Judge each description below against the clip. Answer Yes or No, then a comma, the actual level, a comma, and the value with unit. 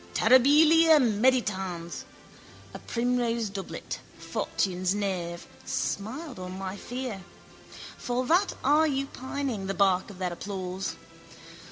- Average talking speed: No, slow, 110 wpm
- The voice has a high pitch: Yes, high, 215 Hz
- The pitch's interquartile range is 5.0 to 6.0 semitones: Yes, wide, 5.5 semitones